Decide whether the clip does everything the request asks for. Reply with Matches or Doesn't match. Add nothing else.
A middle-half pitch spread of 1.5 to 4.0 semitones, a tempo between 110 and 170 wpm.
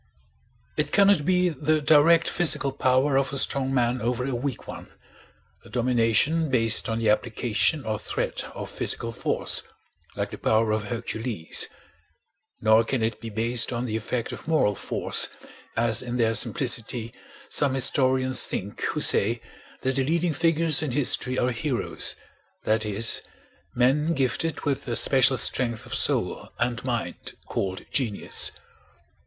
Matches